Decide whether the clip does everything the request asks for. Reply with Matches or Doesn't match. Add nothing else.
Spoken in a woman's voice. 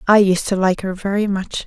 Matches